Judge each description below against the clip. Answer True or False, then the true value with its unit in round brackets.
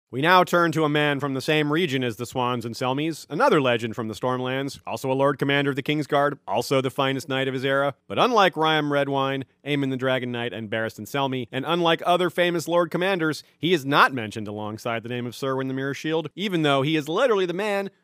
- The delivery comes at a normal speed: False (235 wpm)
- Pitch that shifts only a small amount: False (3.8 semitones)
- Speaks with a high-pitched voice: False (140 Hz)